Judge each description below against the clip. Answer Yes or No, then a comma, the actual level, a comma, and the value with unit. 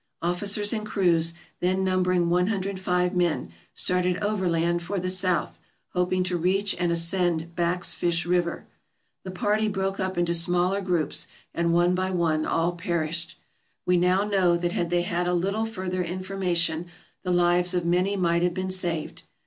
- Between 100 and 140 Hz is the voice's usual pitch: No, medium, 180 Hz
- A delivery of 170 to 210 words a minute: No, average, 160 wpm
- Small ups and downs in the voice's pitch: Yes, narrow, 1.5 semitones